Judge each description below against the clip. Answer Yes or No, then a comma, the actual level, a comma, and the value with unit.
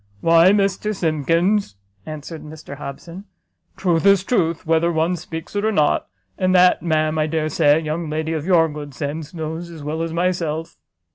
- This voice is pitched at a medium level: Yes, medium, 165 Hz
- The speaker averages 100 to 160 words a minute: No, average, 180 wpm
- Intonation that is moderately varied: No, narrow, 2.3 semitones